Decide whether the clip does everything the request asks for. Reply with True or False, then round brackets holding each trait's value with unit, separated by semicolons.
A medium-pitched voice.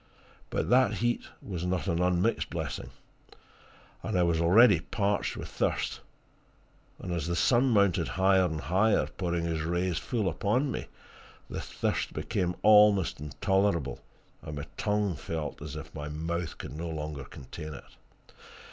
False (90 Hz)